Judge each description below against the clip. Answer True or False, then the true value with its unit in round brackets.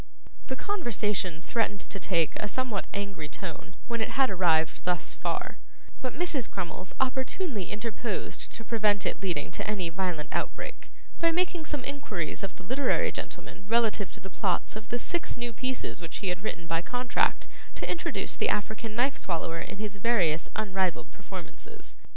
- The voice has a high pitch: True (210 Hz)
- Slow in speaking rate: False (170 wpm)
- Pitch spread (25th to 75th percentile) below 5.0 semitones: False (5.3 semitones)